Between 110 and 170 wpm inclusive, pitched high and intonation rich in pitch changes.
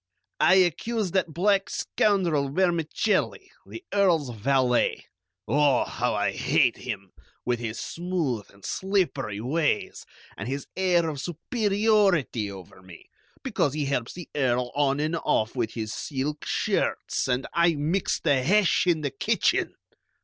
No: average, 140 wpm; medium, 150 Hz; wide, 6.4 semitones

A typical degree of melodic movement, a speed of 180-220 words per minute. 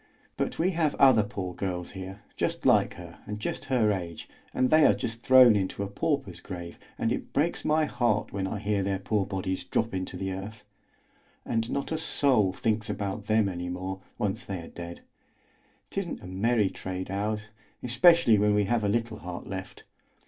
Yes: average, 3.9 semitones; average, 190 wpm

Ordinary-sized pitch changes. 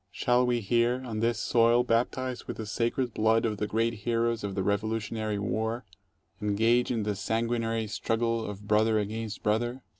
No: narrow, 1.7 semitones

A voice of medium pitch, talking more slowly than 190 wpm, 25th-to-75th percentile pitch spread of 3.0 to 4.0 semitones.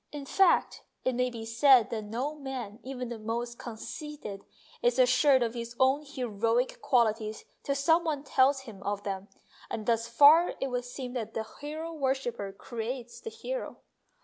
No: very high, 250 Hz; average, 170 wpm; average, 3.5 semitones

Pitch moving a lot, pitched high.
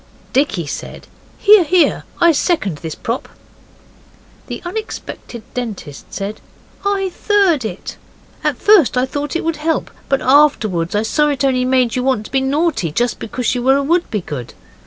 Yes: wide, 6.9 semitones; very high, 265 Hz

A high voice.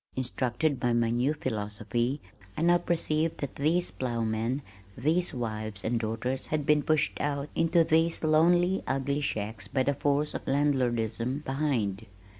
No: low, 135 Hz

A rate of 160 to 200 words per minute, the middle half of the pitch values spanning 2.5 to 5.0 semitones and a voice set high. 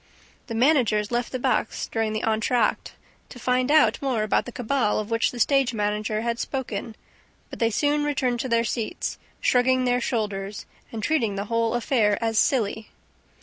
Yes: average, 175 wpm; average, 2.8 semitones; high, 230 Hz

